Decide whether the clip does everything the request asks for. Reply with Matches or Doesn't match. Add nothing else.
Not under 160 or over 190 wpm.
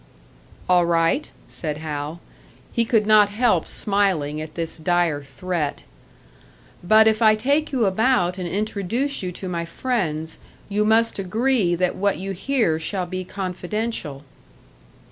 Doesn't match